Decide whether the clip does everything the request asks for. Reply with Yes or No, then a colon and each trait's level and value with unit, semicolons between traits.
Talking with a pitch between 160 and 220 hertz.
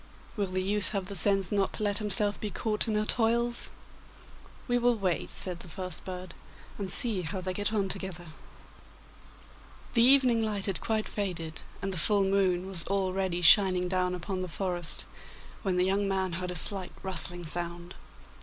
Yes: high, 190 Hz